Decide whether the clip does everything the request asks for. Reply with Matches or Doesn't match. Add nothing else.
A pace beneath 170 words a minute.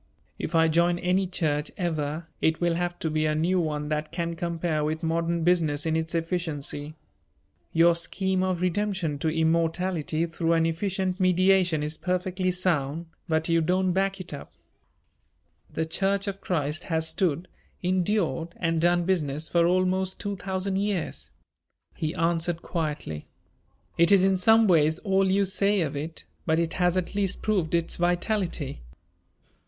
Matches